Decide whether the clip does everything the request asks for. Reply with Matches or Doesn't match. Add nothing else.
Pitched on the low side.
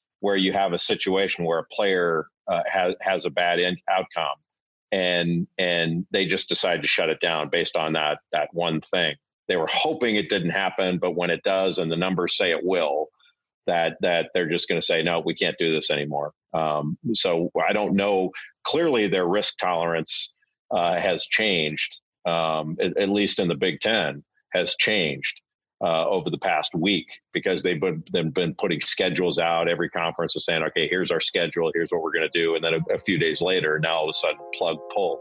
Matches